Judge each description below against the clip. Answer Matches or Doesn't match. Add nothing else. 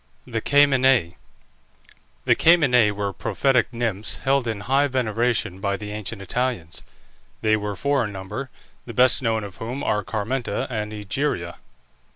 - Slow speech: Doesn't match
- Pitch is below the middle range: Matches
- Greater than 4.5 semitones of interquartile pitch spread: Doesn't match